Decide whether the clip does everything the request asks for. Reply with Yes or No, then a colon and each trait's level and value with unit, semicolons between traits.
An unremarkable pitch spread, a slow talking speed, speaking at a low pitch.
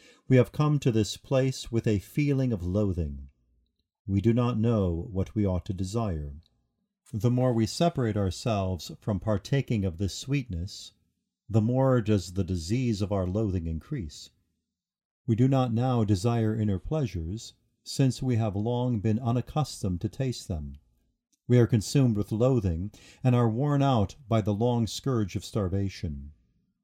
No: average, 4.5 semitones; average, 155 wpm; low, 110 Hz